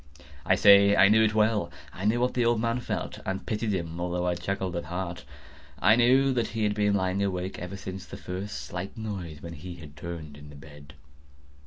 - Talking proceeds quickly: Yes, fast, 215 wpm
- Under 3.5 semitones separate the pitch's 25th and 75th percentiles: No, average, 3.8 semitones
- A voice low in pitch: Yes, very low, 95 Hz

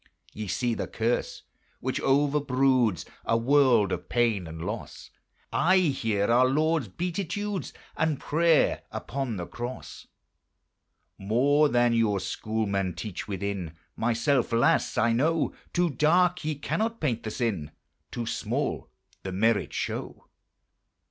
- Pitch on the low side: Yes, low, 120 Hz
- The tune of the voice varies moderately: No, wide, 5.8 semitones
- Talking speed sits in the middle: No, slow, 125 wpm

